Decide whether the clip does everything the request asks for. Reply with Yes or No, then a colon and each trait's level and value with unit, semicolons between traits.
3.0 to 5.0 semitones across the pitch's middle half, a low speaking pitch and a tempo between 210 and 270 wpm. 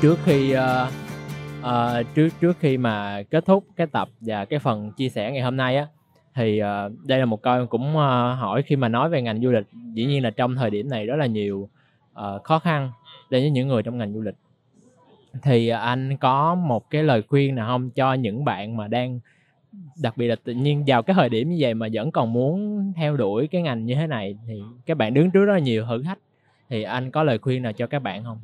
Yes: average, 4.2 semitones; low, 125 Hz; average, 240 wpm